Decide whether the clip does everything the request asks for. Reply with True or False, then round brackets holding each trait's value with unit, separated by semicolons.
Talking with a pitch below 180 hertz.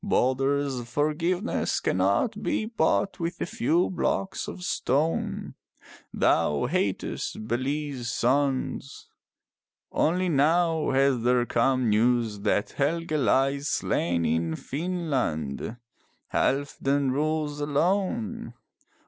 True (140 Hz)